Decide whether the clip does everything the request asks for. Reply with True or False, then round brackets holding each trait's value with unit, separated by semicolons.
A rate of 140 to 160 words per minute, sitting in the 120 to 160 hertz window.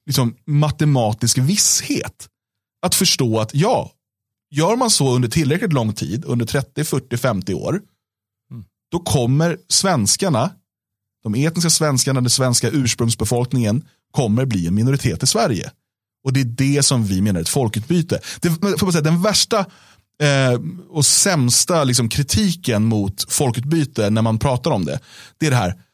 True (150 wpm; 135 Hz)